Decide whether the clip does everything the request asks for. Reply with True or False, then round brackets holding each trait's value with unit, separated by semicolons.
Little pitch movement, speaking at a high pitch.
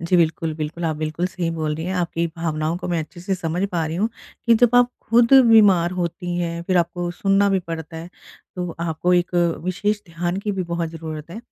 False (2.1 semitones; 175 Hz)